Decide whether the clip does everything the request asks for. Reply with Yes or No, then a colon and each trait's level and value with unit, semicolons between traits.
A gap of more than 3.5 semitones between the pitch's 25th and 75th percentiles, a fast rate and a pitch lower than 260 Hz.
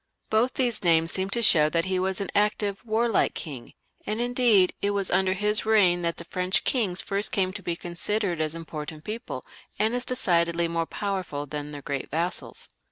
No: average, 4.0 semitones; average, 190 wpm; medium, 185 Hz